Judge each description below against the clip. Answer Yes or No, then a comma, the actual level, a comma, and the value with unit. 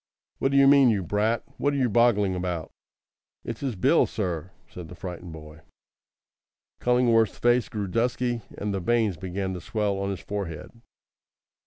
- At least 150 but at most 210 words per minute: Yes, average, 160 wpm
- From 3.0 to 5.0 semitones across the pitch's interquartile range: Yes, average, 4.7 semitones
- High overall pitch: No, low, 105 Hz